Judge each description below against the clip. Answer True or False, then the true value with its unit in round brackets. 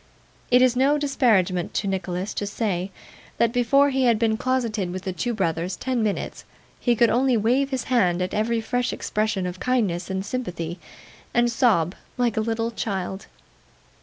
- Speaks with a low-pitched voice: False (225 Hz)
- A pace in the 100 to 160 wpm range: False (170 wpm)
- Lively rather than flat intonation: False (4.7 semitones)